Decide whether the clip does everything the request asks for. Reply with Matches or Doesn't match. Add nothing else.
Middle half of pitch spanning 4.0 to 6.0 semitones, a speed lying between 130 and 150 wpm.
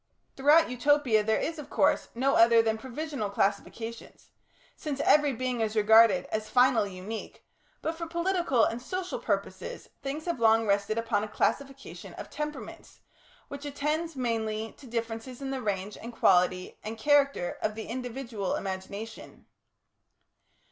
Matches